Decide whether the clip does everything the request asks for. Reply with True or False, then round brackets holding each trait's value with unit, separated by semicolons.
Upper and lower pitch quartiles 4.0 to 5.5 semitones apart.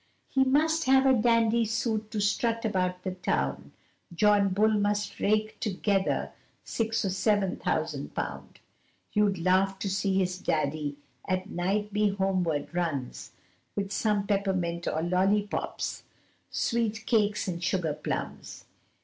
False (2.9 semitones)